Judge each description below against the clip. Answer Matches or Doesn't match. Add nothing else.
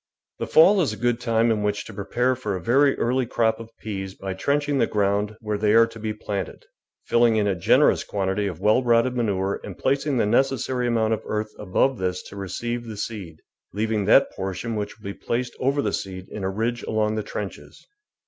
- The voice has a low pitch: Matches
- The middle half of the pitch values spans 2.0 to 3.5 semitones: Matches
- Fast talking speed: Matches